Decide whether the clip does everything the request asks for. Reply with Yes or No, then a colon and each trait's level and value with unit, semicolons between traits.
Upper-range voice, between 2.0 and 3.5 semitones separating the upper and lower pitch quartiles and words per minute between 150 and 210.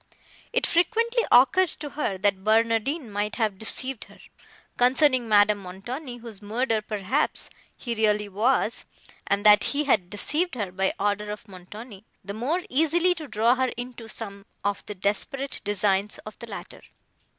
No: high, 220 Hz; average, 4.4 semitones; average, 155 wpm